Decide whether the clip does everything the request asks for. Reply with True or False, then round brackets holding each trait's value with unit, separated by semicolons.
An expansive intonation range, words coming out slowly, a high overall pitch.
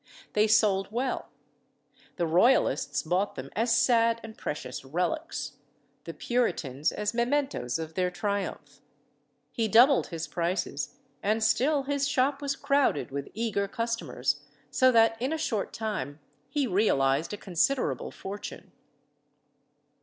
True (6.4 semitones; 130 wpm; 220 Hz)